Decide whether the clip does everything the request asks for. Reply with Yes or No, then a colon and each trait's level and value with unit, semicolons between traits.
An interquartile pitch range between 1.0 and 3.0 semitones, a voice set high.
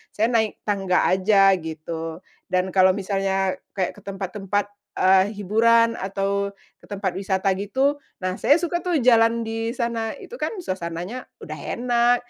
No: average, 3.5 semitones; high, 200 Hz